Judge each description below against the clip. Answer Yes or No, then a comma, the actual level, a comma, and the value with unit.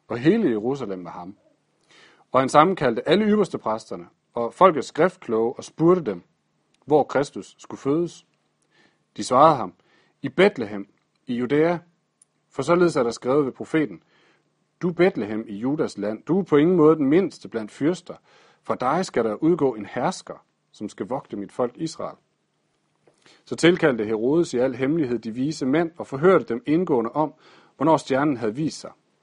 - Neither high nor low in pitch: Yes, medium, 145 Hz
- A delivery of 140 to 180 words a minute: Yes, average, 165 wpm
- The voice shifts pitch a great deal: Yes, wide, 6.0 semitones